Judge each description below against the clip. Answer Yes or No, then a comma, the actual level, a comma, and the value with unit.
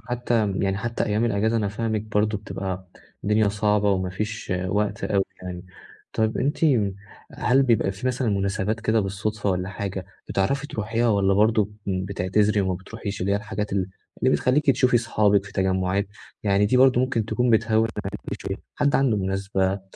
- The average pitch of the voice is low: Yes, low, 105 Hz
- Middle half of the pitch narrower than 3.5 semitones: Yes, narrow, 2.6 semitones